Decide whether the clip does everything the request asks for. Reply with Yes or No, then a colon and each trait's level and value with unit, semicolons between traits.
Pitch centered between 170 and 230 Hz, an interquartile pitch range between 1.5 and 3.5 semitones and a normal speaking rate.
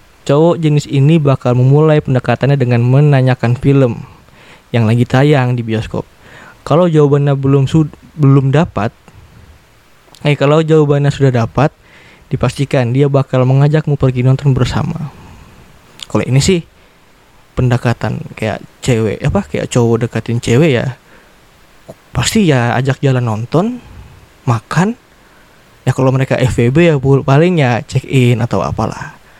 No: low, 135 Hz; average, 3.2 semitones; average, 120 wpm